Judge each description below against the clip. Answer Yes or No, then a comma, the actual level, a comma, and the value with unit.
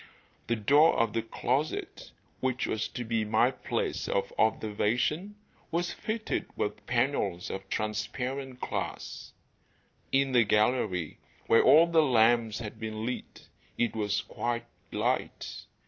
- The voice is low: Yes, low, 115 Hz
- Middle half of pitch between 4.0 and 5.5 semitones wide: No, average, 3.6 semitones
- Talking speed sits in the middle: No, slow, 130 wpm